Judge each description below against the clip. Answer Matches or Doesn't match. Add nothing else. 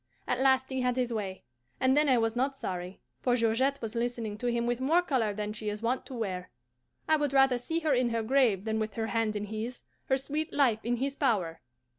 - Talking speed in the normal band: Doesn't match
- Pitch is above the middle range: Matches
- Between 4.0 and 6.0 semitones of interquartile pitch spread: Doesn't match